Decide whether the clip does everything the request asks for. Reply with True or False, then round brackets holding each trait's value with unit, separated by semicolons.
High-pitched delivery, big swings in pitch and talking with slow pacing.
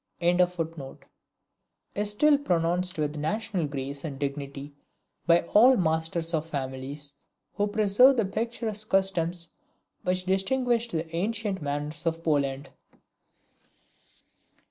False (170 Hz; 5.8 semitones; 110 wpm)